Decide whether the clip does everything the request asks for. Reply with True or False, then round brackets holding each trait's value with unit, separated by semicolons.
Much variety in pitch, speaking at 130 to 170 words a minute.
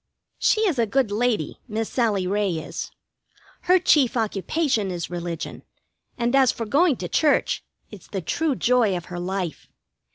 True (6.1 semitones; 160 wpm)